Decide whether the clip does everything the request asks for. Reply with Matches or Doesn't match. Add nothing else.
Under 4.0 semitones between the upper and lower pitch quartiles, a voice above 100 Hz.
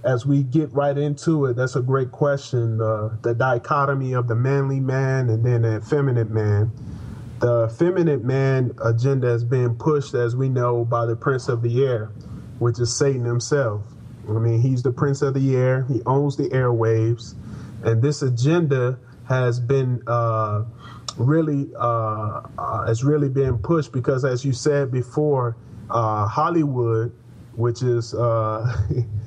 Matches